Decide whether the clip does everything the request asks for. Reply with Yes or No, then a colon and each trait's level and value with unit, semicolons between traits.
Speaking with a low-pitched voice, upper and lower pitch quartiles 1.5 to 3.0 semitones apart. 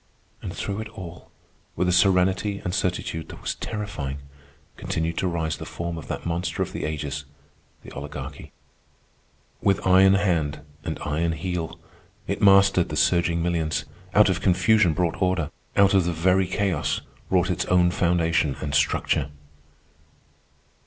Yes: very low, 90 Hz; average, 2.7 semitones